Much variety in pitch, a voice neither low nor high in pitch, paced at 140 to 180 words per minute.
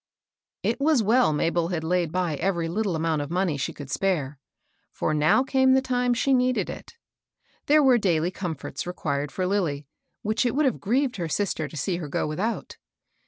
No: wide, 7.4 semitones; medium, 180 Hz; average, 195 wpm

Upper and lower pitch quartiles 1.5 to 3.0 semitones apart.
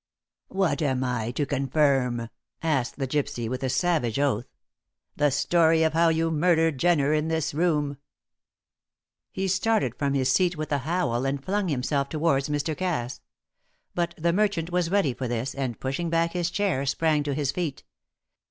No: average, 4.0 semitones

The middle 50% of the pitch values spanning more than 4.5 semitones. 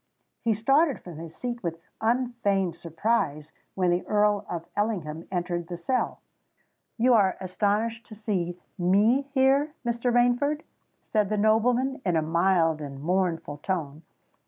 Yes: wide, 5.6 semitones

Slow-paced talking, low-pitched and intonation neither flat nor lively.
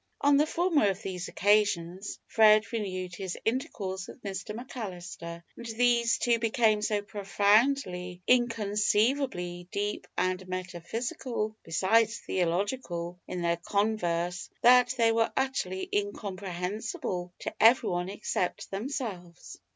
No: slow, 110 wpm; high, 205 Hz; average, 4.1 semitones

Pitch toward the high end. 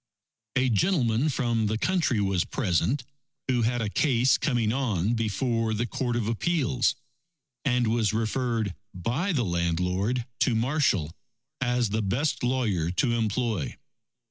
No: low, 115 Hz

